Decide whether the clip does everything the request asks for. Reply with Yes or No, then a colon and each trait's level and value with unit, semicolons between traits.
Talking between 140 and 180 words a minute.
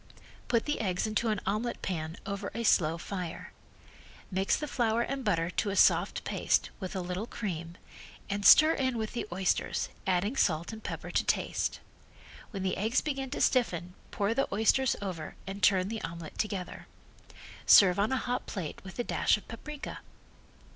Yes: average, 175 wpm